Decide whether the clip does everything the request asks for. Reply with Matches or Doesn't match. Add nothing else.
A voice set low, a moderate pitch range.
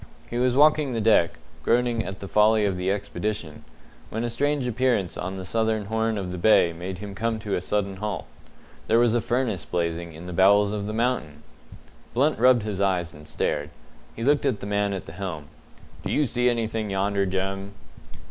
Matches